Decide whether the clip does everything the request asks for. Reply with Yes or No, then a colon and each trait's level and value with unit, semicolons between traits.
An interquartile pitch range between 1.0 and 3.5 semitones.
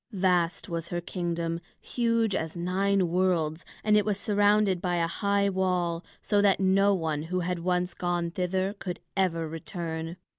Yes: average, 2.7 semitones